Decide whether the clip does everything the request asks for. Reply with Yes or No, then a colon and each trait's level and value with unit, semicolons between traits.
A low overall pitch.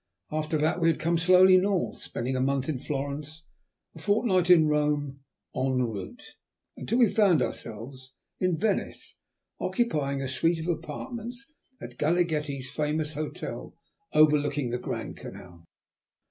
No: medium, 155 Hz